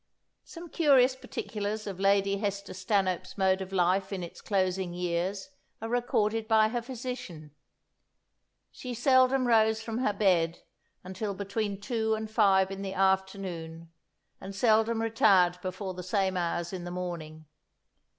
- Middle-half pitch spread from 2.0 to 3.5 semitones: Yes, average, 3.2 semitones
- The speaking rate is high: No, average, 140 wpm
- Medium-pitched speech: No, high, 195 Hz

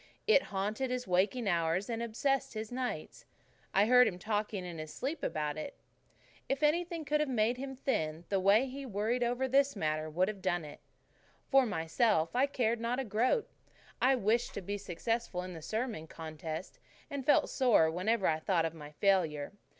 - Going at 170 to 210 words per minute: Yes, average, 190 wpm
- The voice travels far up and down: Yes, wide, 6.5 semitones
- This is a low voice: No, high, 215 Hz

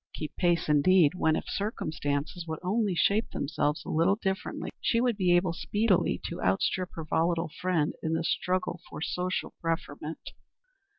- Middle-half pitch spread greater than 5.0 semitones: No, average, 2.9 semitones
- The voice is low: No, medium, 175 Hz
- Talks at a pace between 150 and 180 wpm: Yes, average, 160 wpm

